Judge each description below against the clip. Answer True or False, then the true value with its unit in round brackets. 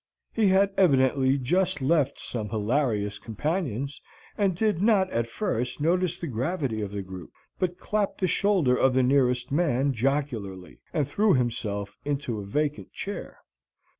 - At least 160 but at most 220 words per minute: False (150 wpm)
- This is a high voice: False (140 Hz)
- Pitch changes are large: True (7.1 semitones)